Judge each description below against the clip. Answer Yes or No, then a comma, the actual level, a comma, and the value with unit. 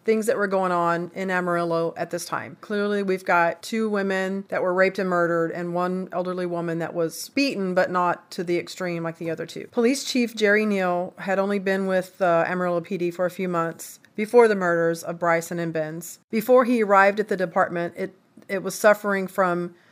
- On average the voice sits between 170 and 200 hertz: Yes, medium, 185 Hz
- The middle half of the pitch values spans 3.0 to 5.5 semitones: No, narrow, 2.6 semitones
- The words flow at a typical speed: No, fast, 210 wpm